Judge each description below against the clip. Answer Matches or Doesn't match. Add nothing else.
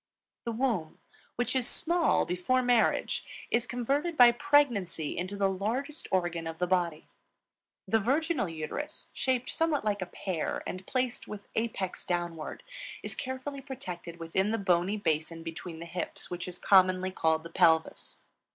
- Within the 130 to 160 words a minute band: Matches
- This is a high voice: Matches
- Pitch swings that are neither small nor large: Doesn't match